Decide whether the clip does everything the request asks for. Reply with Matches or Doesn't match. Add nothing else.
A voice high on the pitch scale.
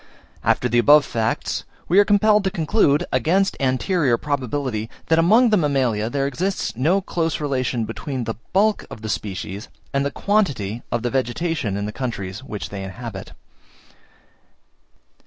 Doesn't match